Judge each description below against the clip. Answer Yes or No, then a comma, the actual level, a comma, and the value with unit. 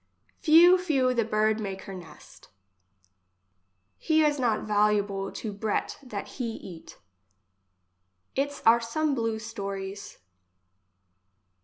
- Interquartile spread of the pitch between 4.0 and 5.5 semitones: Yes, average, 5.0 semitones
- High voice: Yes, high, 225 Hz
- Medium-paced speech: No, slow, 110 wpm